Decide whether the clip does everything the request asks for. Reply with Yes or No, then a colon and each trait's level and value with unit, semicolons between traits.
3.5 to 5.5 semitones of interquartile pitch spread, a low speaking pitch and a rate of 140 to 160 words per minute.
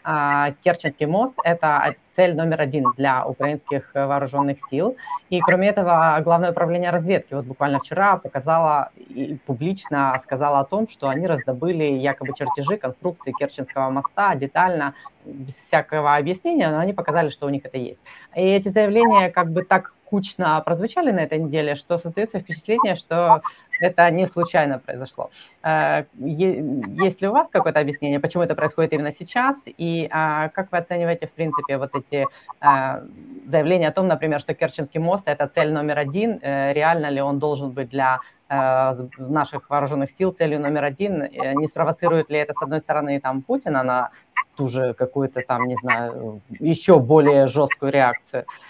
No: average, 4.2 semitones; medium, 155 Hz; fast, 155 wpm